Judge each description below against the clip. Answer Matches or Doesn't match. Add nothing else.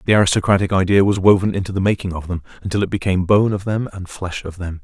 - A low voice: Matches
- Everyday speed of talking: Doesn't match